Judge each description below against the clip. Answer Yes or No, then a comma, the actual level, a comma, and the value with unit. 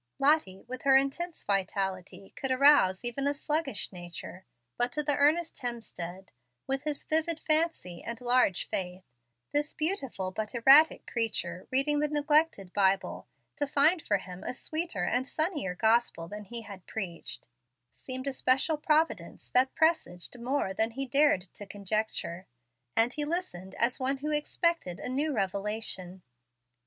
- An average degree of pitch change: No, wide, 7.3 semitones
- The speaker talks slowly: No, average, 150 wpm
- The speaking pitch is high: Yes, very high, 250 Hz